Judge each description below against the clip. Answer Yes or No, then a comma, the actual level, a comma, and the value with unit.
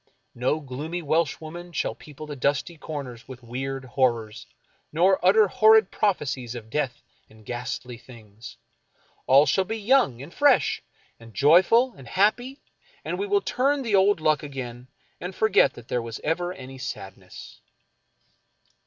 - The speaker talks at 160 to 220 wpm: No, average, 150 wpm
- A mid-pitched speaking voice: Yes, medium, 145 Hz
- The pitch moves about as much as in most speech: No, wide, 7.3 semitones